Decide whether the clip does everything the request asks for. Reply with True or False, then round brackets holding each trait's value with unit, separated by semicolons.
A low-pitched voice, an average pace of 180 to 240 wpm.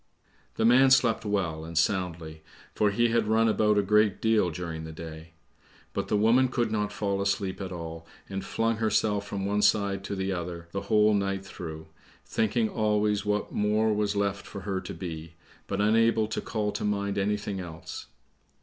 True (100 Hz; 185 wpm)